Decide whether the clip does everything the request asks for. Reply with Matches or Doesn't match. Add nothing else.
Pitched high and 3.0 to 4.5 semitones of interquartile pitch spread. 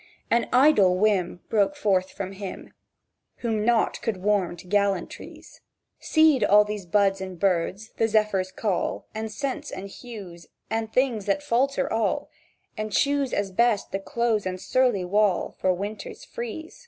Matches